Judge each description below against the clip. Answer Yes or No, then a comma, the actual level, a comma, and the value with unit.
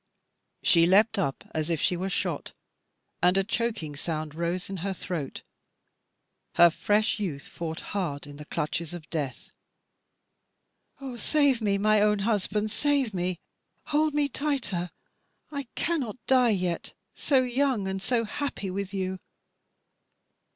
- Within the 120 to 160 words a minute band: Yes, average, 140 wpm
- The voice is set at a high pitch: Yes, high, 195 Hz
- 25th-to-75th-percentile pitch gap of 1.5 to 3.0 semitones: No, wide, 5.5 semitones